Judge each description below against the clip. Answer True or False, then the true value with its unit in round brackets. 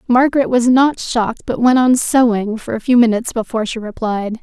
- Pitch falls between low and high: False (235 Hz)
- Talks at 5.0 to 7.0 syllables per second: True (5.7 syllables/s)